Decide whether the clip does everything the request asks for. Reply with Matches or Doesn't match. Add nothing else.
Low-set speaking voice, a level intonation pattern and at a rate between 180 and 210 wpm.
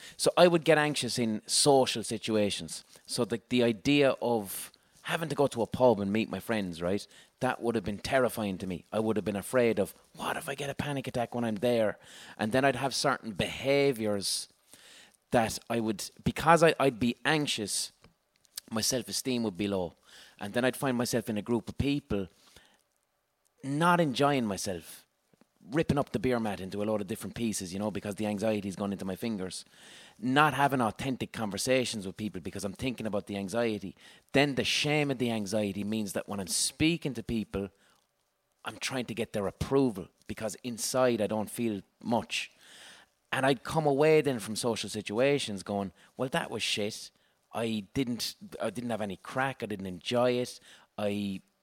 Doesn't match